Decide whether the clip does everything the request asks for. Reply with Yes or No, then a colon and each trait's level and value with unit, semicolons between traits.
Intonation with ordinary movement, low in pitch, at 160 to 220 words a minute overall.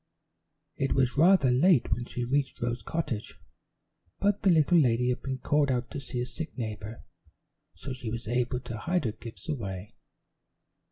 Yes: average, 3.7 semitones; low, 125 Hz; average, 170 wpm